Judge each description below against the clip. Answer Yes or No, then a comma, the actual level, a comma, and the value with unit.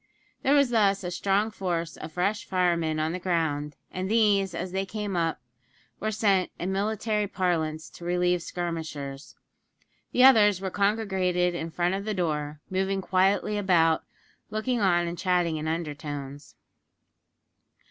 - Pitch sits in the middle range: Yes, medium, 180 Hz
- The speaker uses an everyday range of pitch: Yes, average, 3.3 semitones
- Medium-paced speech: Yes, average, 145 wpm